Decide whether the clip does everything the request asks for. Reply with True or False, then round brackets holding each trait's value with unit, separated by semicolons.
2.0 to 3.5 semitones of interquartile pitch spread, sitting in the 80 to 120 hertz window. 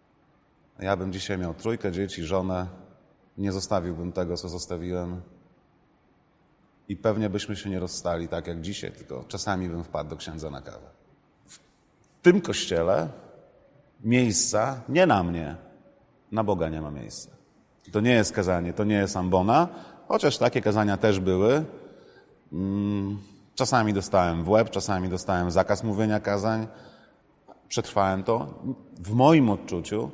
True (3.2 semitones; 100 Hz)